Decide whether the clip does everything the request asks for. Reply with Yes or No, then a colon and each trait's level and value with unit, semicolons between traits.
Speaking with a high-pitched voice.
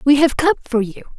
Yes: very high, 275 Hz